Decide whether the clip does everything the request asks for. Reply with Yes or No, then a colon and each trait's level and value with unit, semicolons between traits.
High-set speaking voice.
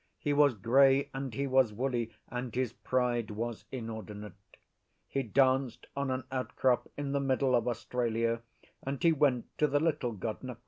No: low, 130 Hz